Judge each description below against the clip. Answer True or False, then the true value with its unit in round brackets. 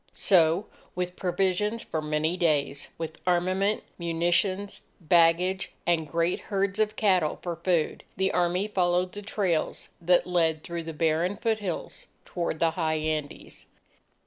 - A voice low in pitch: False (175 Hz)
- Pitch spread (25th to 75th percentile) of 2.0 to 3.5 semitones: True (2.7 semitones)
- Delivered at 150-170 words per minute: False (135 wpm)